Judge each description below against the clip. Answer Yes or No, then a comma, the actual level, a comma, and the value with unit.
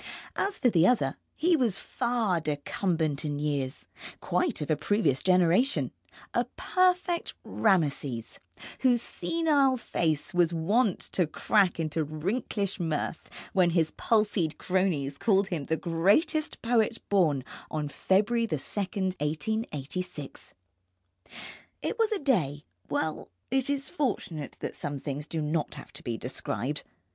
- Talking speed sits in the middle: No, slow, 130 wpm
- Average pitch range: No, wide, 7.4 semitones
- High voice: No, medium, 180 Hz